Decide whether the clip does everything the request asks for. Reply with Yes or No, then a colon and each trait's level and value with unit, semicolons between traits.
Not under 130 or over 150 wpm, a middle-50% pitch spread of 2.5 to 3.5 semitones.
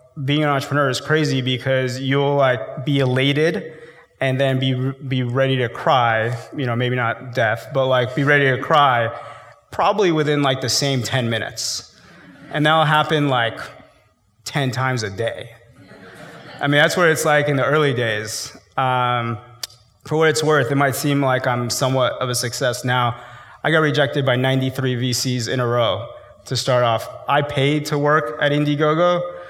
No: average, 175 wpm; average, 2.9 semitones